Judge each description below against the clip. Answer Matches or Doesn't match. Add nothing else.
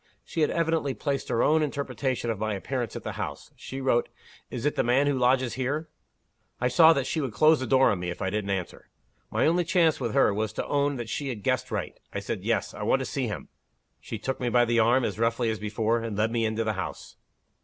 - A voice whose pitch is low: Matches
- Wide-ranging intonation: Doesn't match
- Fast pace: Matches